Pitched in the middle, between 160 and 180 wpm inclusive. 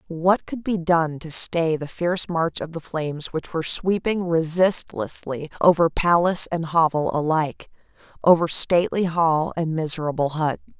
No: medium, 165 Hz; average, 150 wpm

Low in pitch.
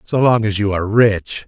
Yes: low, 105 Hz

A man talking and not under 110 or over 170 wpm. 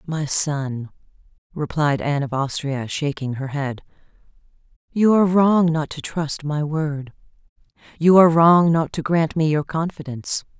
No: female; average, 145 wpm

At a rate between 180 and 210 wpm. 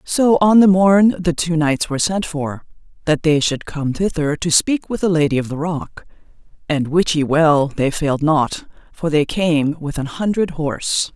Yes: average, 200 wpm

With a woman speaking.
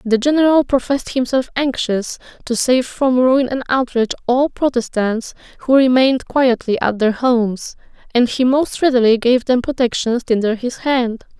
Yes: female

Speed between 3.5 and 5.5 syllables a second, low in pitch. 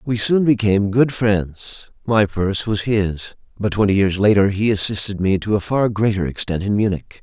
Yes: 5.3 syllables/s; low, 105 Hz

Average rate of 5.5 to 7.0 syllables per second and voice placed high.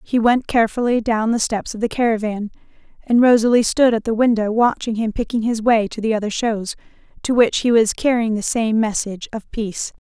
Yes: 5.6 syllables/s; high, 225 Hz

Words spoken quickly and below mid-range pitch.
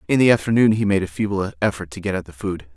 Yes: fast, 285 wpm; very low, 95 Hz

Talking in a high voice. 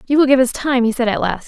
Yes: high, 245 Hz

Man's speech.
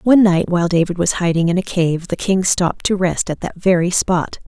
No: female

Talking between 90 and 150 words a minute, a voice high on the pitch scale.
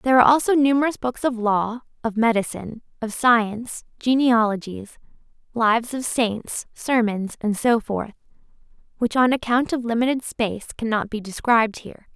Yes: average, 145 wpm; high, 235 Hz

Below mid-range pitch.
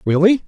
No: high, 190 Hz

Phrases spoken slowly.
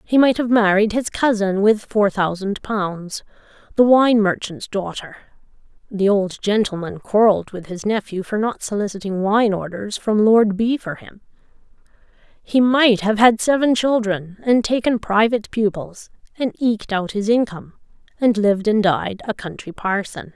No: average, 155 wpm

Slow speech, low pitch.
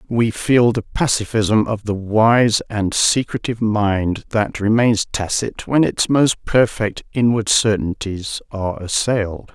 Yes: slow, 130 wpm; low, 110 Hz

